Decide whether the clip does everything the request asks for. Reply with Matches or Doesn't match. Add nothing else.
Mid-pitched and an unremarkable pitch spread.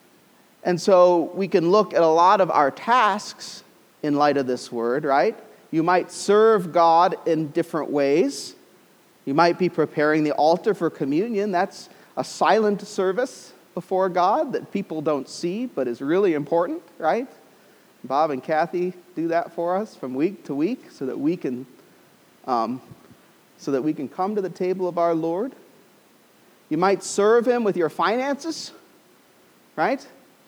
Matches